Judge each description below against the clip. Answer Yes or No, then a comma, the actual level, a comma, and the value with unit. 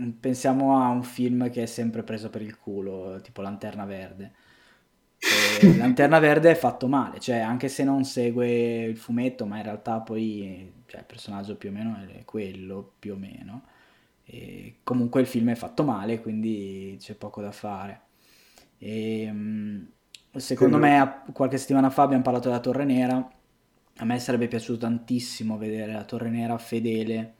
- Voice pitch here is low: Yes, low, 115 Hz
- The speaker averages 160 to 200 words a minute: Yes, average, 165 wpm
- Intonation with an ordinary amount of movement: Yes, average, 3.0 semitones